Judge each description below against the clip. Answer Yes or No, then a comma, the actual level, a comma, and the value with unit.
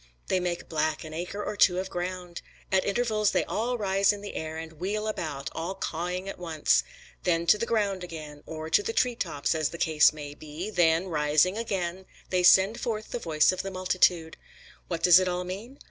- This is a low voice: No, medium, 180 Hz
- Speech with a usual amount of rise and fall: Yes, average, 3.7 semitones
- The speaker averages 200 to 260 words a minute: Yes, fast, 205 wpm